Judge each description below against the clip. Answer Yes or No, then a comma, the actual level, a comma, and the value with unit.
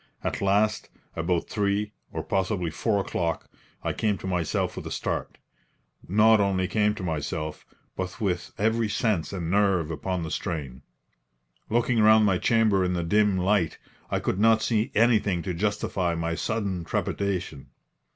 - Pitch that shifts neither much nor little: Yes, average, 3.5 semitones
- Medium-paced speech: Yes, average, 155 wpm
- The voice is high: No, very low, 95 Hz